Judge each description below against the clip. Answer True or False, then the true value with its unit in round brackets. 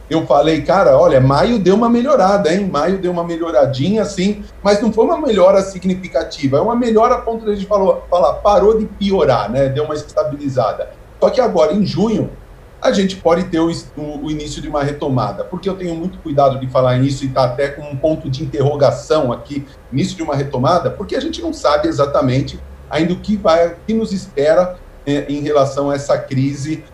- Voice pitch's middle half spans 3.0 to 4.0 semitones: False (5.6 semitones)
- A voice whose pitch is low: False (160 Hz)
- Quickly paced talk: True (205 wpm)